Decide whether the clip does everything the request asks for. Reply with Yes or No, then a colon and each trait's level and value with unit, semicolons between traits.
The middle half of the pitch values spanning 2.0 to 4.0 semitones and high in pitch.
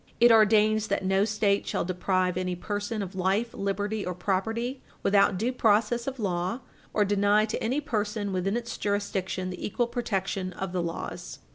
Yes: average, 2.9 semitones; high, 205 Hz